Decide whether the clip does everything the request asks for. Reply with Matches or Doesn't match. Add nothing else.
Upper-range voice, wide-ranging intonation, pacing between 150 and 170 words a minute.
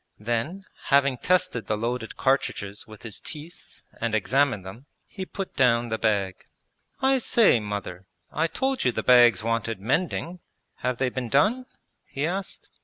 Doesn't match